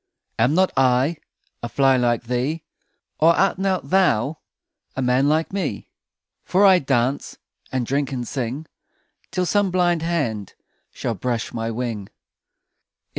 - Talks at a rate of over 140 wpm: No, slow, 135 wpm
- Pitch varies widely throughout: Yes, wide, 5.9 semitones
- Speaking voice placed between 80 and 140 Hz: Yes, low, 135 Hz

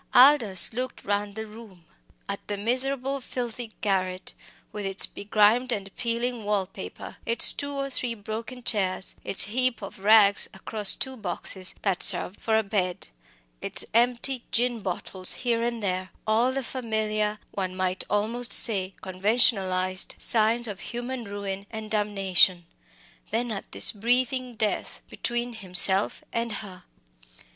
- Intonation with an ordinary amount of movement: Yes, average, 3.6 semitones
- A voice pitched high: Yes, high, 215 Hz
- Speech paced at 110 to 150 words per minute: Yes, average, 140 wpm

